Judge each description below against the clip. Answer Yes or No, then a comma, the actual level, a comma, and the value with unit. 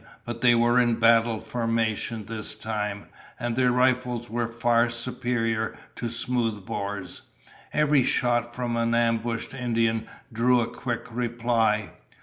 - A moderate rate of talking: No, slow, 130 wpm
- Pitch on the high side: No, low, 115 Hz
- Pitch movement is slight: Yes, narrow, 1.2 semitones